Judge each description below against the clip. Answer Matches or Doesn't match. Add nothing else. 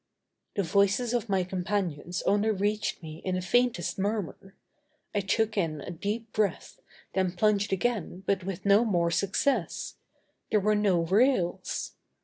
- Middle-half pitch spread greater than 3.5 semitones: Doesn't match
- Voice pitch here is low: Doesn't match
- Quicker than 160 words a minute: Doesn't match